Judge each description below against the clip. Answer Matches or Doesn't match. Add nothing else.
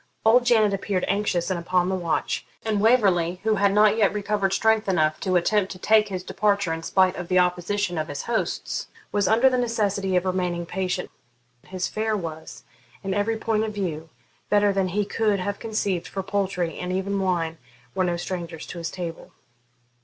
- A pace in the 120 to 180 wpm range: Doesn't match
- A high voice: Matches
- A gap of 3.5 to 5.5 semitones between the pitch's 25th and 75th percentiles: Doesn't match